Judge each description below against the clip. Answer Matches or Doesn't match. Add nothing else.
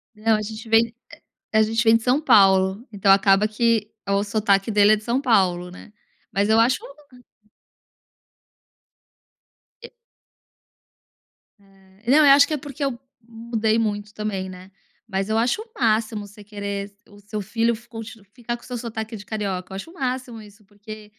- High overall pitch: Matches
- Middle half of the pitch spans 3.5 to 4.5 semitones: Doesn't match